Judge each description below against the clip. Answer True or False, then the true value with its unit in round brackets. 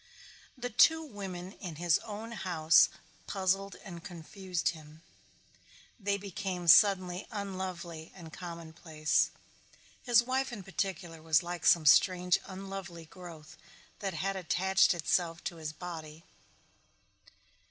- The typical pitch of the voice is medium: True (180 Hz)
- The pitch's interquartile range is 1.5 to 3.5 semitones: True (2.9 semitones)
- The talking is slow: True (115 wpm)